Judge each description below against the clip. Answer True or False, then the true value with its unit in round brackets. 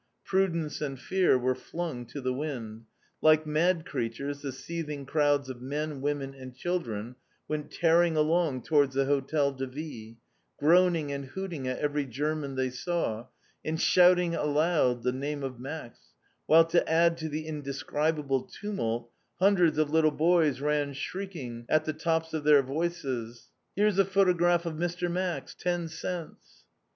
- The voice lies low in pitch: False (150 Hz)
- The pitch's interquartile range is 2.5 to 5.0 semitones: True (4.0 semitones)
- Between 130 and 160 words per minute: True (155 wpm)